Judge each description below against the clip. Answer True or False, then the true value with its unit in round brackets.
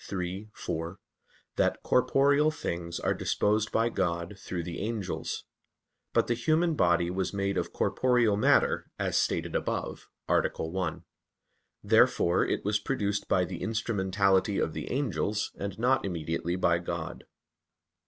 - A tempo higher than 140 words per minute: False (135 wpm)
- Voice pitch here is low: True (100 Hz)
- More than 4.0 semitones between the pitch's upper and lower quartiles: True (4.5 semitones)